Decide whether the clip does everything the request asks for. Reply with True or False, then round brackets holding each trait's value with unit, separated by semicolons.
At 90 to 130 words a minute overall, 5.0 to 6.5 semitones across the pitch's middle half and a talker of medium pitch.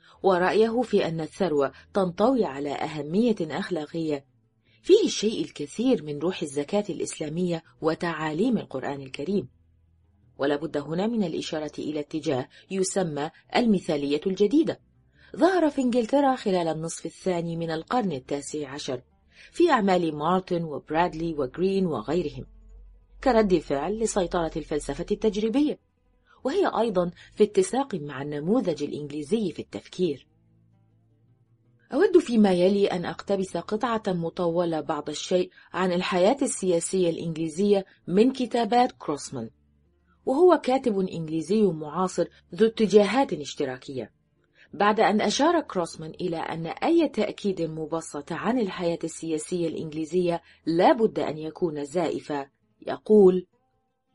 True (110 wpm; 5.6 semitones; 175 Hz)